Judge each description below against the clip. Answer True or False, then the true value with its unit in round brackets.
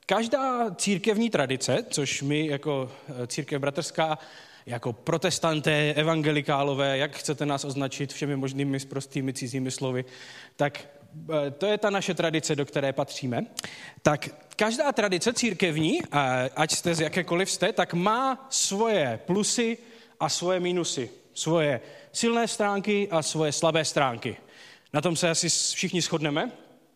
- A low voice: False (155 Hz)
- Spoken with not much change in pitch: False (4.9 semitones)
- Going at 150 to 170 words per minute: False (130 wpm)